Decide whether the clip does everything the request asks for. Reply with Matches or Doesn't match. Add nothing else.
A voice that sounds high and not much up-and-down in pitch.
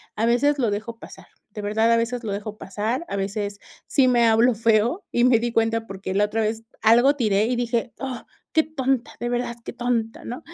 Matches